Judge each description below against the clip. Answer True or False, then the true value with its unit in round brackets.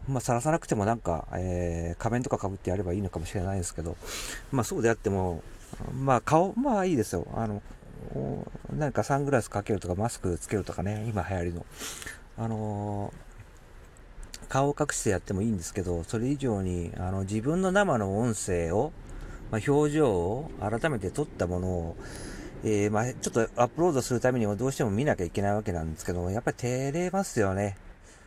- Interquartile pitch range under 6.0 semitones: True (5.4 semitones)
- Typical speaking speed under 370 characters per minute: False (390 characters per minute)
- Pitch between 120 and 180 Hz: False (105 Hz)